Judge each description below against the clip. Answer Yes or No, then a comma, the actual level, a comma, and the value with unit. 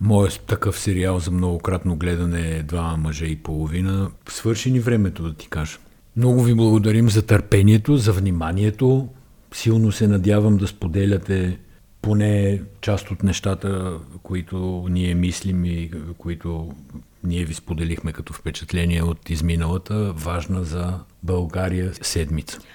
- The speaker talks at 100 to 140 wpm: Yes, average, 130 wpm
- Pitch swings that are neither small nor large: Yes, average, 3.4 semitones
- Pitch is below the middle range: Yes, very low, 90 Hz